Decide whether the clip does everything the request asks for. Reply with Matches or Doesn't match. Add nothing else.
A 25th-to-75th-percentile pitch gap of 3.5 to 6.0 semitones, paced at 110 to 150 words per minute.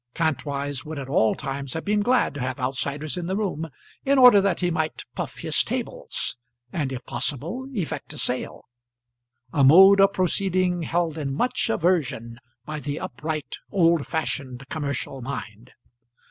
Doesn't match